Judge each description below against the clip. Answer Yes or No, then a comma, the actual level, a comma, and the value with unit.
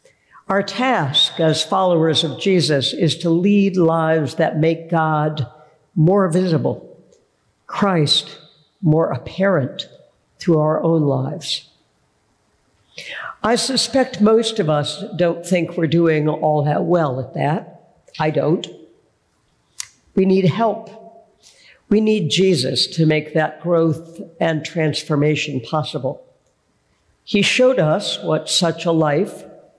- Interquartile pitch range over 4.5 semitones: No, average, 4.0 semitones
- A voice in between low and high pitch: Yes, medium, 165 Hz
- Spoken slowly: Yes, slow, 115 wpm